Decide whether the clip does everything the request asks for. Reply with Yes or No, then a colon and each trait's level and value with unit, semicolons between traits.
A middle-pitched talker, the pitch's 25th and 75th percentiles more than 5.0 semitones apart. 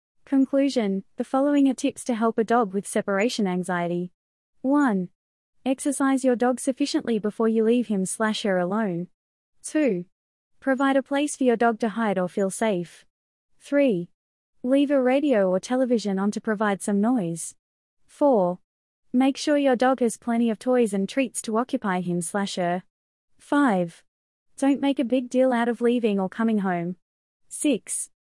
No: high, 230 Hz; wide, 5.4 semitones